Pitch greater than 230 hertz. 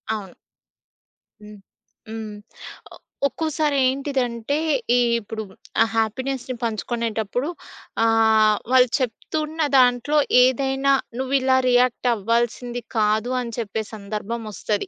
Yes: high, 240 Hz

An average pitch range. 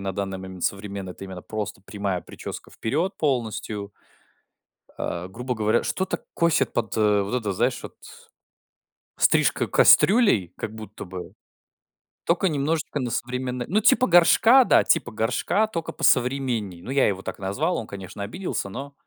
No: wide, 6.6 semitones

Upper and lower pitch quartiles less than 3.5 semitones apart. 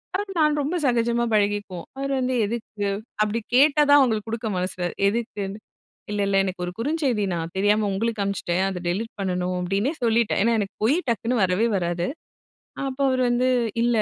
No: average, 4.0 semitones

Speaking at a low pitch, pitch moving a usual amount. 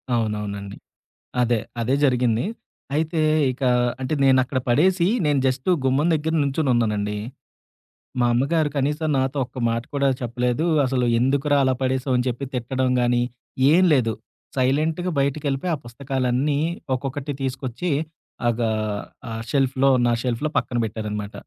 Yes: low, 130 Hz; average, 3.0 semitones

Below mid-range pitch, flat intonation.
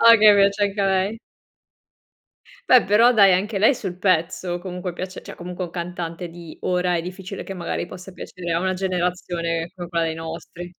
No: medium, 180 Hz; narrow, 2.0 semitones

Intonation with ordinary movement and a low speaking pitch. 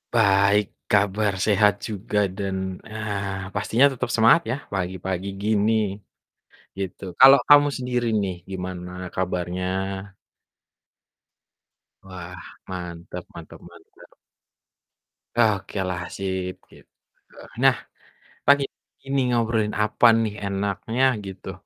Yes: average, 3.1 semitones; low, 100 Hz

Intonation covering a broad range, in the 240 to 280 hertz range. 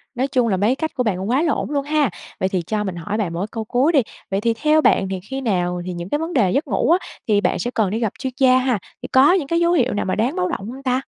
Yes: wide, 5.8 semitones; high, 245 Hz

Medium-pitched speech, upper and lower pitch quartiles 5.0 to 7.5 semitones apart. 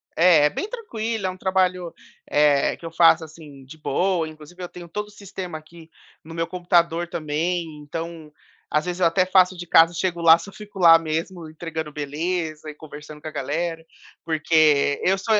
No: medium, 165 Hz; narrow, 2.6 semitones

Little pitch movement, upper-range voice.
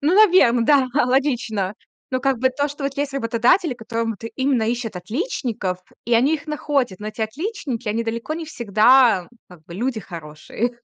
No: average, 4.3 semitones; high, 245 Hz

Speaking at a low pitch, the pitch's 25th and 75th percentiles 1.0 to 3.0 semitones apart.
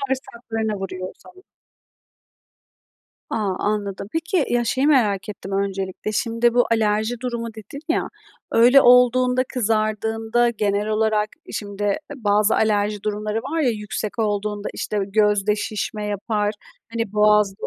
No: high, 215 Hz; narrow, 2.4 semitones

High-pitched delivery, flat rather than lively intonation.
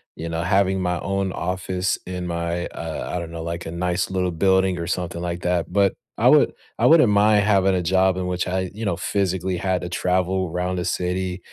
No: very low, 90 Hz; narrow, 1.4 semitones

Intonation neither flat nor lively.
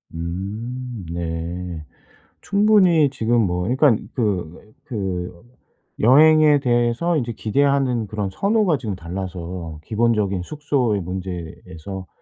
No: wide, 6.6 semitones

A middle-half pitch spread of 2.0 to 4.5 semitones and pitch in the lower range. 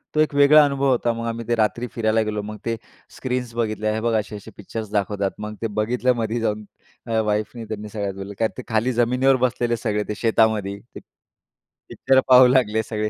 Yes: narrow, 2.5 semitones; low, 115 Hz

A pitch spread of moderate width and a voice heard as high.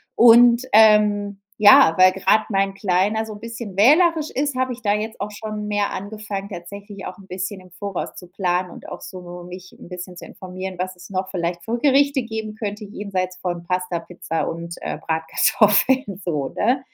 Yes: average, 3.2 semitones; high, 200 Hz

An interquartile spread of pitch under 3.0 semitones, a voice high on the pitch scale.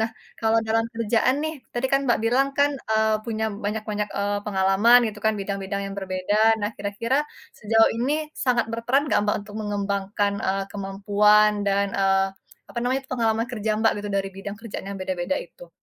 Yes: narrow, 2.5 semitones; high, 210 Hz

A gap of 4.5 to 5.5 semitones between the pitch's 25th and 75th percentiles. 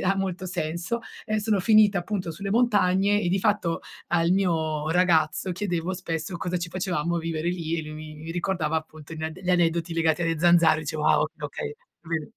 No: average, 2.8 semitones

